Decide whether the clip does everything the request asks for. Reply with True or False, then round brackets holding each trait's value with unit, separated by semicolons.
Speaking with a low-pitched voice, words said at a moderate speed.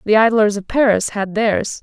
False (210 Hz; 195 wpm)